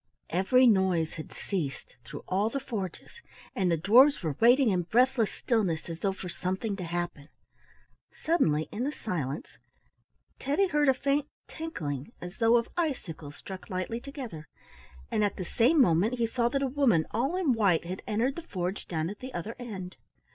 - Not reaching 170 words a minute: No, average, 175 wpm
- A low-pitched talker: No, high, 210 Hz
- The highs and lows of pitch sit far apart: Yes, wide, 6.8 semitones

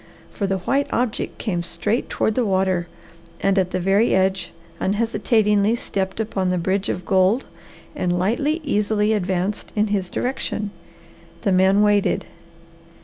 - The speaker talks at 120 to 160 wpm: Yes, average, 145 wpm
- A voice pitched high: Yes, high, 200 Hz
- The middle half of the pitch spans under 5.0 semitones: Yes, narrow, 2.5 semitones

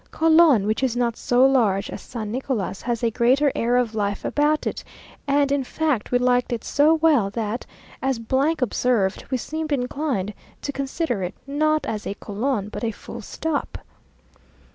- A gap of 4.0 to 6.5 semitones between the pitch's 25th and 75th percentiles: Yes, average, 4.5 semitones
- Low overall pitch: No, very high, 250 Hz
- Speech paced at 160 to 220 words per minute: Yes, average, 170 wpm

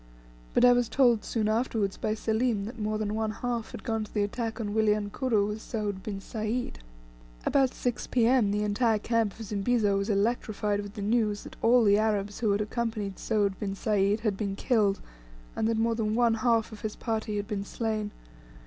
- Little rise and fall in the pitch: Yes, narrow, 1.9 semitones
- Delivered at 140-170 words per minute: No, average, 200 wpm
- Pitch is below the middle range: No, high, 215 Hz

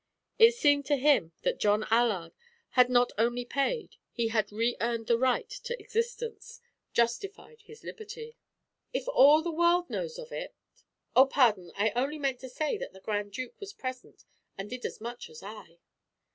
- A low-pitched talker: No, very high, 255 Hz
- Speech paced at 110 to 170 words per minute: No, average, 180 wpm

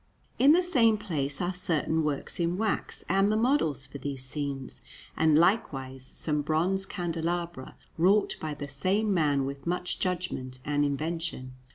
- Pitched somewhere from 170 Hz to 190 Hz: No, medium, 160 Hz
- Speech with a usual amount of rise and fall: Yes, average, 4.9 semitones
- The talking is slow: No, average, 155 wpm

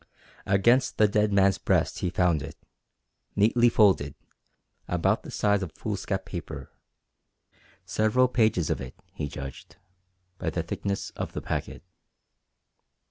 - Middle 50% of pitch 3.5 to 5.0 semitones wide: Yes, average, 4.4 semitones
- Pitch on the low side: Yes, very low, 95 Hz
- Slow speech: Yes, slow, 130 wpm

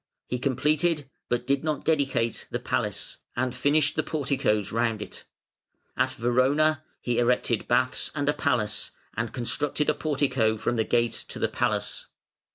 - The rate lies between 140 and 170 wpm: Yes, average, 155 wpm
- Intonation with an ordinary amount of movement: Yes, average, 3.5 semitones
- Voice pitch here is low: Yes, low, 130 Hz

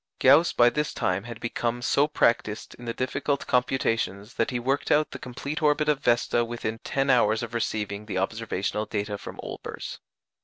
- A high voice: No, low, 120 Hz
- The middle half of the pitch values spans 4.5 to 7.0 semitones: No, average, 3.9 semitones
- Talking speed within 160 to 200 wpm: Yes, average, 180 wpm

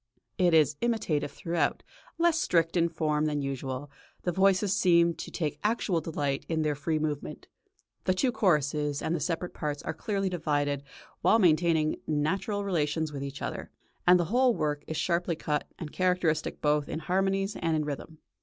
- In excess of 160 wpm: Yes, average, 175 wpm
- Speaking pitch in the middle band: Yes, medium, 160 Hz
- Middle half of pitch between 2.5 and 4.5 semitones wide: Yes, average, 3.7 semitones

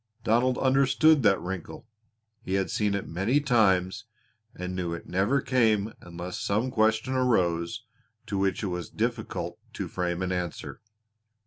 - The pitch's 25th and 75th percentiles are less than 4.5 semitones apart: No, average, 4.9 semitones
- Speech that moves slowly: No, average, 145 wpm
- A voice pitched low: Yes, low, 100 Hz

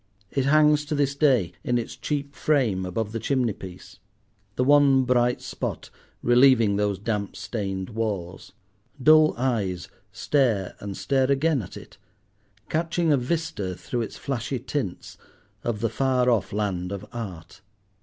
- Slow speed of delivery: No, average, 145 wpm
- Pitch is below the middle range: Yes, low, 120 Hz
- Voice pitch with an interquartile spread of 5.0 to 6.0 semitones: Yes, wide, 5.4 semitones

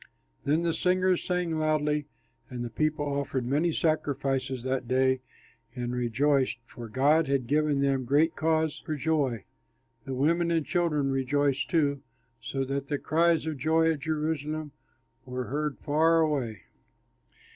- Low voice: No, medium, 145 Hz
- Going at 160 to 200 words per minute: No, average, 145 wpm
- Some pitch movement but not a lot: Yes, average, 3.1 semitones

